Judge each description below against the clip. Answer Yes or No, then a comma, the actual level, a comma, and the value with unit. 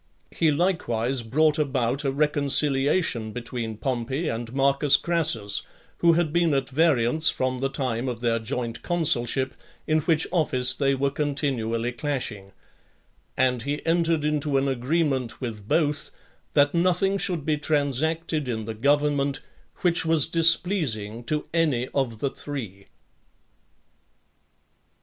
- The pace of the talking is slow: Yes, slow, 130 wpm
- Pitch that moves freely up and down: No, average, 4.3 semitones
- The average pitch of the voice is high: No, medium, 140 Hz